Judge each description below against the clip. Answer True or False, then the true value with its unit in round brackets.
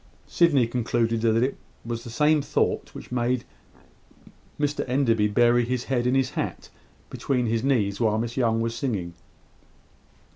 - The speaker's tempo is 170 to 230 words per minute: False (150 wpm)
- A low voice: True (120 Hz)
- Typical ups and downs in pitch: False (2.3 semitones)